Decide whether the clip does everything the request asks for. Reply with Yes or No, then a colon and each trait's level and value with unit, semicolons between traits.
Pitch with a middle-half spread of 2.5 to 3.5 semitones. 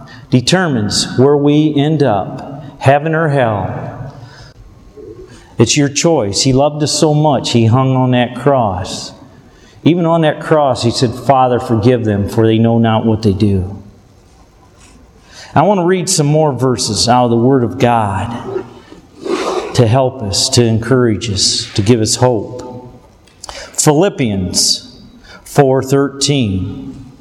No: average, 4.0 semitones